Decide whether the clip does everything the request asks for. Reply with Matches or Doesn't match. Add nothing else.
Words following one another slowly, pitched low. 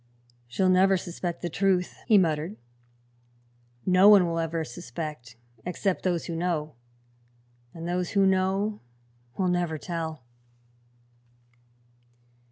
Doesn't match